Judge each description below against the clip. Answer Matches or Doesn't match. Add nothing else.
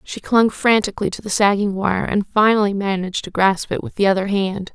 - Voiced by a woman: Matches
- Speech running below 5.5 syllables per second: Doesn't match